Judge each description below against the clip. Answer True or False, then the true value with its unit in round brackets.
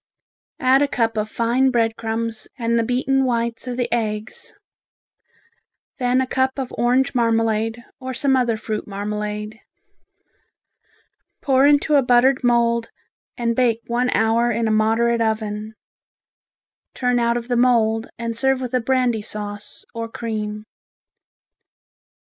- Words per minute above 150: False (135 wpm)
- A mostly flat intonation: True (2.2 semitones)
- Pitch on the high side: True (235 Hz)